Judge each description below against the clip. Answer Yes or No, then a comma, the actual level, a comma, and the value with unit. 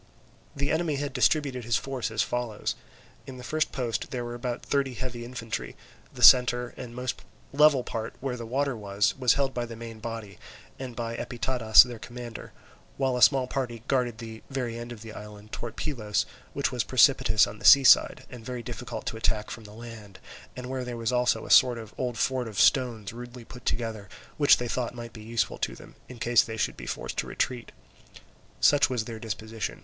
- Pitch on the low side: Yes, low, 120 Hz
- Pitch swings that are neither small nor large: No, narrow, 2.1 semitones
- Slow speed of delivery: No, fast, 205 wpm